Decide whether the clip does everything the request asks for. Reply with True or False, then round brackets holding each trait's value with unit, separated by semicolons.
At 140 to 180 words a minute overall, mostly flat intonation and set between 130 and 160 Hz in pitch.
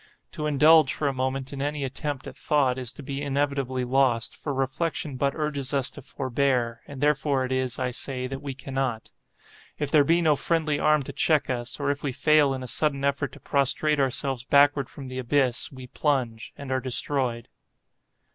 False (195 wpm; 2.0 semitones; 135 Hz)